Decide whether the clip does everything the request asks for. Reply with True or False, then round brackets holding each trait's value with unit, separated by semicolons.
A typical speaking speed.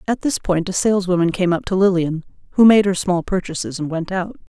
False (220 wpm)